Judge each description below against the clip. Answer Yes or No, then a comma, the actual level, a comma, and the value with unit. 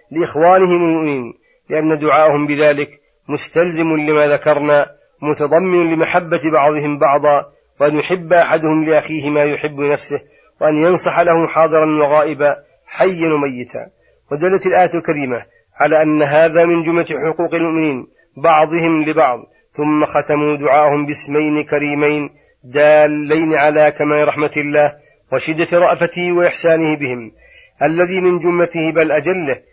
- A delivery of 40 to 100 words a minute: No, average, 115 wpm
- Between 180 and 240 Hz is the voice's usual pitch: No, medium, 155 Hz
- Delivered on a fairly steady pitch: Yes, narrow, 2.2 semitones